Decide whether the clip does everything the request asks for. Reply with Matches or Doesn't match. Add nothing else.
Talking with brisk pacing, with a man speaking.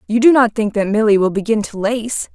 Doesn't match